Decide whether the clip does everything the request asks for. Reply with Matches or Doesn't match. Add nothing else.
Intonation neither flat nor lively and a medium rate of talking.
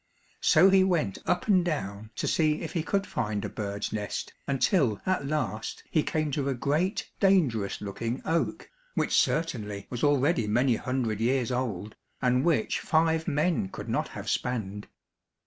Doesn't match